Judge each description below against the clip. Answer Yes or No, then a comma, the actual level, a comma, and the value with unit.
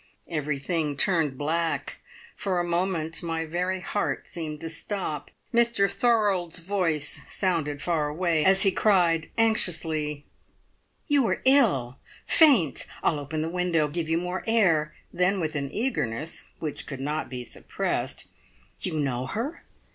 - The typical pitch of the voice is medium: Yes, medium, 165 Hz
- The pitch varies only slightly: No, average, 4.0 semitones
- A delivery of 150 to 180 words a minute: No, average, 140 wpm